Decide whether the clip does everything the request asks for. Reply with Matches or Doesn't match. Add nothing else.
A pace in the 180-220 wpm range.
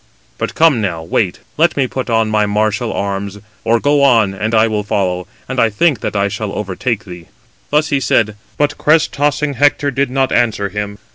Matches